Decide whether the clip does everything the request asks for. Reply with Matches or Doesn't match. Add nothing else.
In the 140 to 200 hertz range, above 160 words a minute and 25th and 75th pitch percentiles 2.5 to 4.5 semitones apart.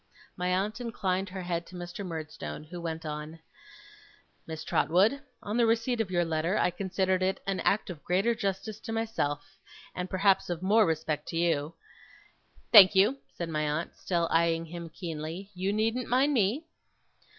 Matches